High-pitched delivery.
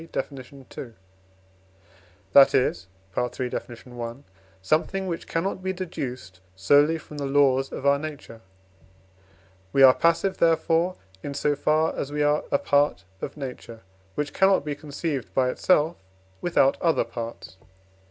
No: medium, 145 Hz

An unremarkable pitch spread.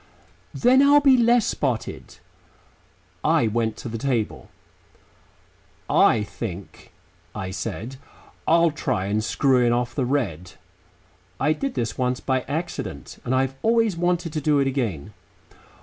No: wide, 7.0 semitones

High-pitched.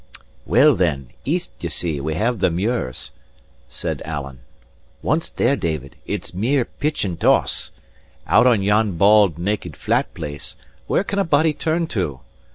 No: low, 100 Hz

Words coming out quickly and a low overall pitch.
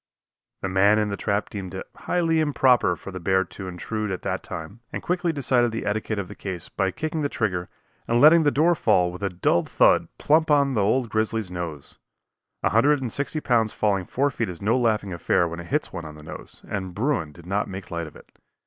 Yes: fast, 230 wpm; low, 105 Hz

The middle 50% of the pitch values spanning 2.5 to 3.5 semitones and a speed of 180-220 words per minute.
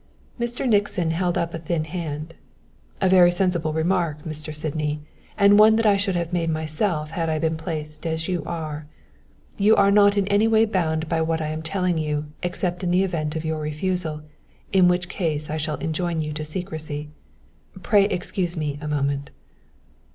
Yes: average, 3.1 semitones; average, 185 wpm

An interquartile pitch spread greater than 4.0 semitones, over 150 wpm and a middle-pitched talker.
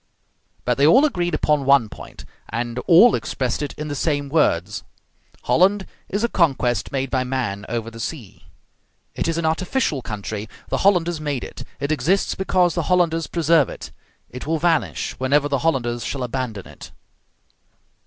Yes: average, 5.2 semitones; average, 165 wpm; medium, 145 Hz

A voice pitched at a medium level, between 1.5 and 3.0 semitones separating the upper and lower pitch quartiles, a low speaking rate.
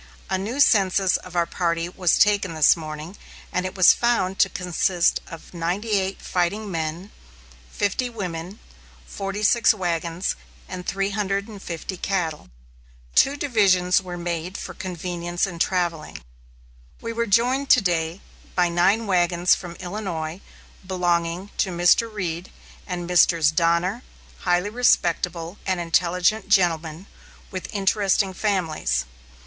Yes: medium, 180 Hz; average, 2.7 semitones; slow, 120 wpm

